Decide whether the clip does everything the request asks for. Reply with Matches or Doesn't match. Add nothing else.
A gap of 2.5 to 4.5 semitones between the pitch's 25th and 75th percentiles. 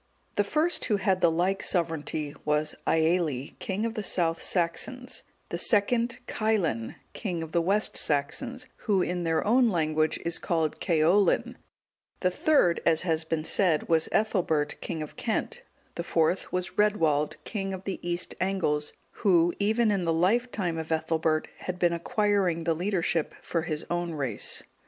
Matches